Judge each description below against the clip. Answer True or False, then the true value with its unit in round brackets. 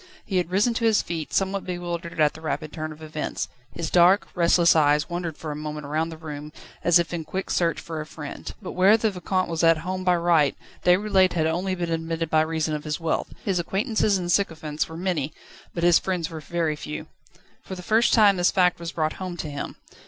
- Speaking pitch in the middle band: True (170 Hz)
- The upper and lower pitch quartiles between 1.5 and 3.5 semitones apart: True (2.8 semitones)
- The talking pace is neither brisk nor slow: False (220 wpm)